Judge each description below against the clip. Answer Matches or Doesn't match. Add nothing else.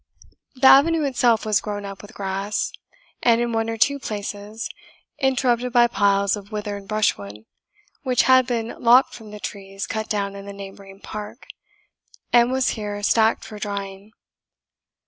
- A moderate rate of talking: Matches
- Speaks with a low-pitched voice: Doesn't match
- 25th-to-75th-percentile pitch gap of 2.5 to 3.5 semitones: Matches